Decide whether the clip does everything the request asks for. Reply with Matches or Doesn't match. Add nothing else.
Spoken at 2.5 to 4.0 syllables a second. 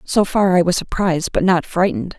Doesn't match